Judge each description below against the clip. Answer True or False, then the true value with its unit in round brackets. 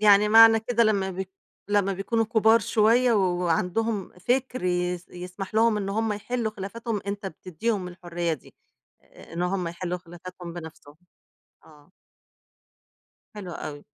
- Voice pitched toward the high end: True (195 Hz)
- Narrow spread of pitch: False (3.8 semitones)